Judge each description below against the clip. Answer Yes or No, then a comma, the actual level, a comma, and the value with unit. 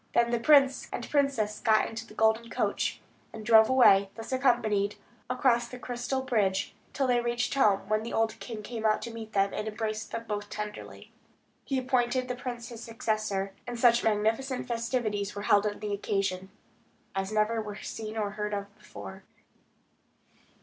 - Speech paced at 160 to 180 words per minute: Yes, average, 175 wpm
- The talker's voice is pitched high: Yes, high, 220 Hz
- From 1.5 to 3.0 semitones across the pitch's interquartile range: Yes, narrow, 2.5 semitones